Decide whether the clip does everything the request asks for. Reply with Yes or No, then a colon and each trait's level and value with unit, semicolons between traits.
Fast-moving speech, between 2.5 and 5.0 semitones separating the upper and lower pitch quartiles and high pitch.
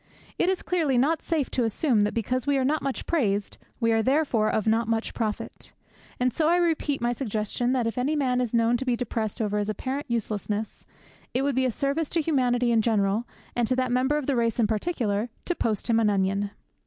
Yes: fast, 225 wpm; average, 3.9 semitones; high, 245 Hz